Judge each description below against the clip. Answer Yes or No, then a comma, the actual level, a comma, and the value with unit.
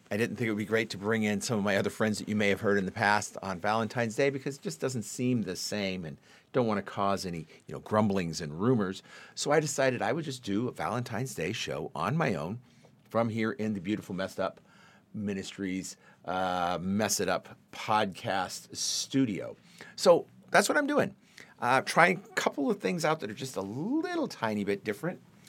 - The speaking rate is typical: No, fast, 215 wpm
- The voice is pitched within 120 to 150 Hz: No, low, 105 Hz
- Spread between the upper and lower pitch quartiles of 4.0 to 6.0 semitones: Yes, average, 4.8 semitones